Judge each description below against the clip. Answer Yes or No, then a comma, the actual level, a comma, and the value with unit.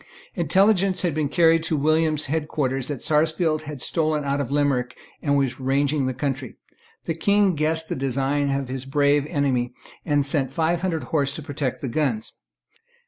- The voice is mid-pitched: Yes, medium, 145 Hz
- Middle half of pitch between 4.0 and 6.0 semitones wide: No, average, 2.8 semitones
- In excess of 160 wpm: Yes, average, 175 wpm